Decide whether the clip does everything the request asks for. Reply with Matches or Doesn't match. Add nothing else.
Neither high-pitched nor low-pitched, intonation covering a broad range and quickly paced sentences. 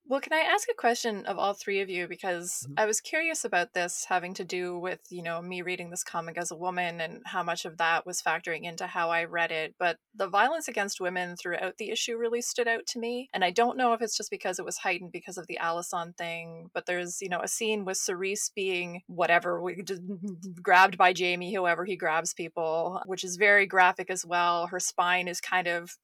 Doesn't match